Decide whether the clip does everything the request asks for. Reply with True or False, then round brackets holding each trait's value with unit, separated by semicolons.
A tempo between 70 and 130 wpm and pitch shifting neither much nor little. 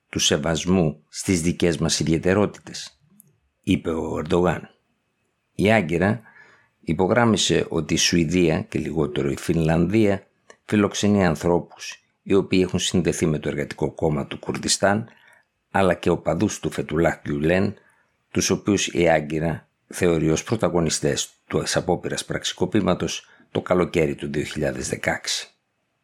True (120 wpm; 3.1 semitones)